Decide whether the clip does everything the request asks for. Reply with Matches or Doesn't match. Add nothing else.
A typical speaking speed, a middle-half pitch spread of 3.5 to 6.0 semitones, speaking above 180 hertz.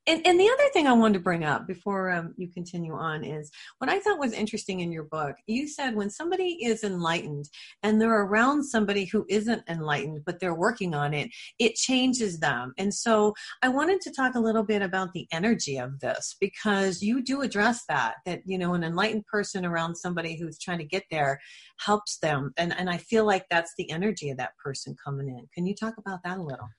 Doesn't match